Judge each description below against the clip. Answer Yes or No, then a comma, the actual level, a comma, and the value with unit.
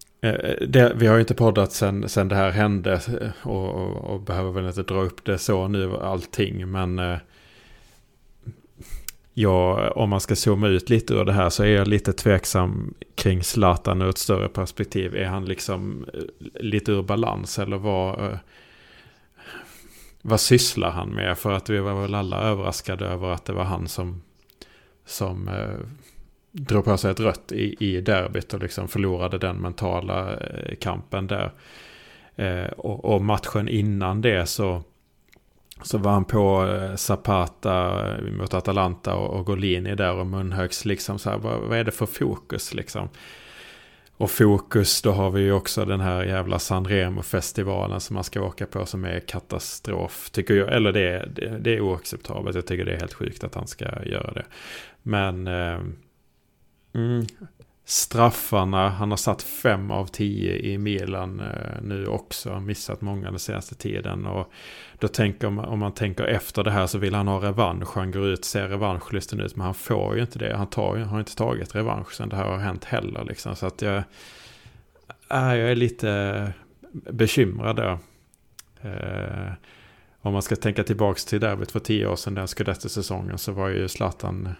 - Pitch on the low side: Yes, low, 100 Hz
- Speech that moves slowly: No, average, 175 wpm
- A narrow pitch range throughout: Yes, narrow, 2.3 semitones